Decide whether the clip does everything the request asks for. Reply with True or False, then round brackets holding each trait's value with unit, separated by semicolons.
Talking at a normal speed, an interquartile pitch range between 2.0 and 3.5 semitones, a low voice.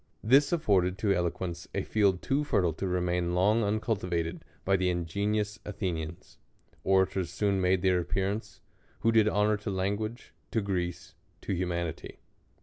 True (145 wpm; 2.9 semitones; 95 Hz)